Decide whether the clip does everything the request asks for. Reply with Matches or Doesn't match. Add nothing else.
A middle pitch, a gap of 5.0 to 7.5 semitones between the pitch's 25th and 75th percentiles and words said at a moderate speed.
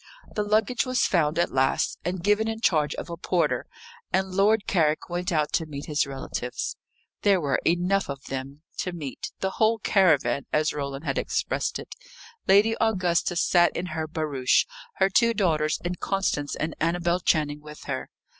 Doesn't match